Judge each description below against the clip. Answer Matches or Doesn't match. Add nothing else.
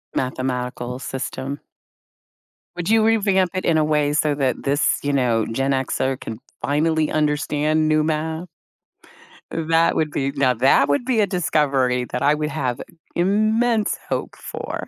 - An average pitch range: Matches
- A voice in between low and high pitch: Matches